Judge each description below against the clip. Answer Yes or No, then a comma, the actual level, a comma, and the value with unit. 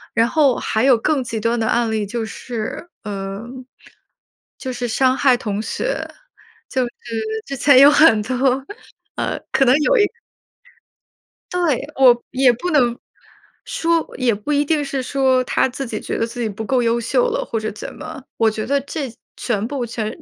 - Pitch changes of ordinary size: Yes, average, 3.7 semitones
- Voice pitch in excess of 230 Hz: Yes, very high, 250 Hz